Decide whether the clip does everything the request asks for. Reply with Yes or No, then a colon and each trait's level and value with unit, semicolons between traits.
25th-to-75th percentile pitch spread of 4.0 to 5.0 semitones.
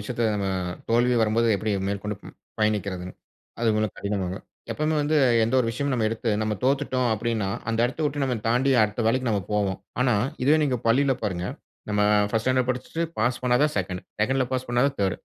No: average, 3.5 semitones